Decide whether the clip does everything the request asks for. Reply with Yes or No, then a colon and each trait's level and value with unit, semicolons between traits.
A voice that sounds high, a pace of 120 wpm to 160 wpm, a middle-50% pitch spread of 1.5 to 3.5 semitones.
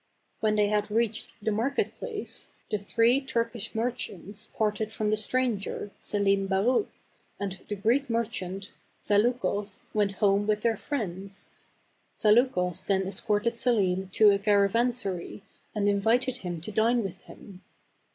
Yes: high, 210 Hz; average, 140 wpm; average, 2.8 semitones